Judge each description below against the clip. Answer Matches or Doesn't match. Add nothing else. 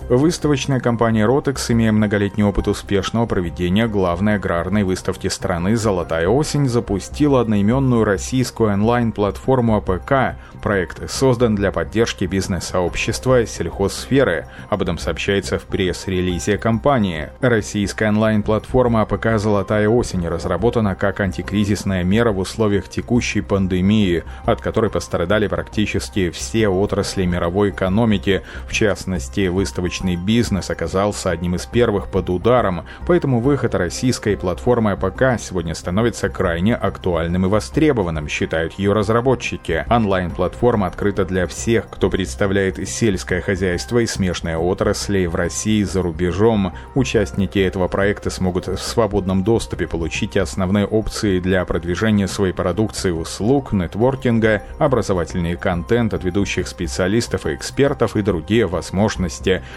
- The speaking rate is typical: Matches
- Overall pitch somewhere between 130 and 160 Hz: Doesn't match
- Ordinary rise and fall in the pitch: Matches